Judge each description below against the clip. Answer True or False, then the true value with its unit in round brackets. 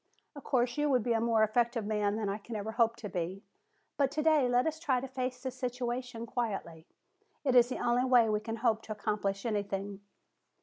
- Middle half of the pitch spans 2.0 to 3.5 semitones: True (3.1 semitones)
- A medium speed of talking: False (210 wpm)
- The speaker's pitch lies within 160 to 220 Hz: False (235 Hz)